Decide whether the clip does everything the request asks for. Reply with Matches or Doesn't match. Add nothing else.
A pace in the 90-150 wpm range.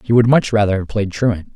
Doesn't match